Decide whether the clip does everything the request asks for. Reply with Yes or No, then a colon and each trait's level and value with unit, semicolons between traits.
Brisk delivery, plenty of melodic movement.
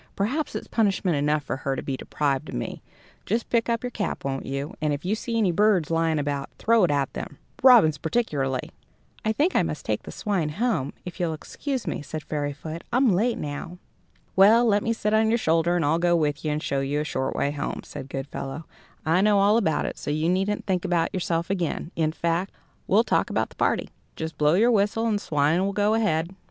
Yes: fast, 225 wpm; wide, 6.1 semitones